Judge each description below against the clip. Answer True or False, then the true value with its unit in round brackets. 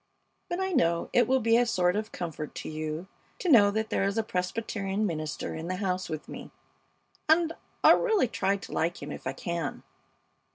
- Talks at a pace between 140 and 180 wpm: False (200 wpm)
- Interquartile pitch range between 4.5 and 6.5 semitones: True (5.1 semitones)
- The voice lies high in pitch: True (195 Hz)